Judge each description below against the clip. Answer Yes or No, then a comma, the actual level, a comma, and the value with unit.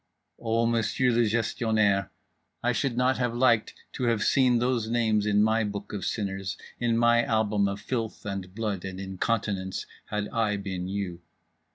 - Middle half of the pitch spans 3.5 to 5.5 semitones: No, average, 2.9 semitones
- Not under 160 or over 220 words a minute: Yes, average, 165 wpm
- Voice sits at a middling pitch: No, low, 110 Hz